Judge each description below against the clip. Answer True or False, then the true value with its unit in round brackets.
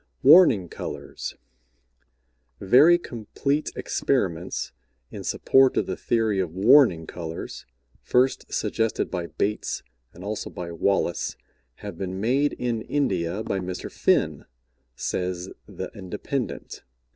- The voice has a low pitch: True (100 Hz)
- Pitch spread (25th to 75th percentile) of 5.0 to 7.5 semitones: True (5.6 semitones)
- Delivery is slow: True (110 wpm)